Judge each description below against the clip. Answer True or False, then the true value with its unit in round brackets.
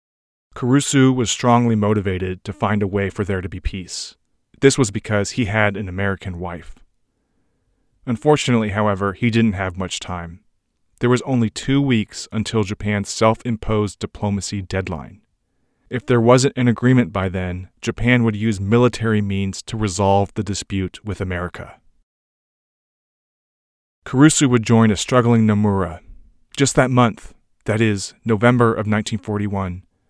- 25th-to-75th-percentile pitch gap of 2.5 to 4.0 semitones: True (3.6 semitones)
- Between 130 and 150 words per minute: True (140 wpm)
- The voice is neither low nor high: False (105 Hz)